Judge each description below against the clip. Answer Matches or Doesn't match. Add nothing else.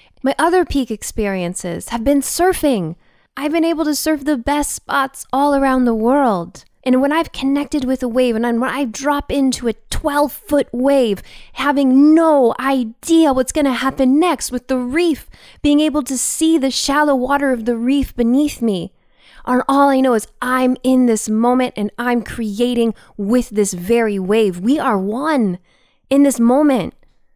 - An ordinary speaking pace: Matches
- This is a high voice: Matches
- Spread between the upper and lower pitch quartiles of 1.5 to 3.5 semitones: Matches